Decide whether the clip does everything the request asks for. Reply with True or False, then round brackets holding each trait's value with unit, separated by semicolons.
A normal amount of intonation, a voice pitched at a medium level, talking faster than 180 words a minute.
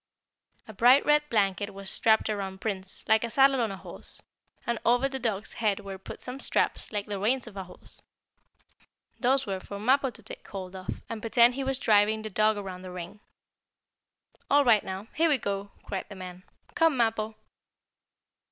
False (3.9 semitones; 215 Hz; 190 wpm)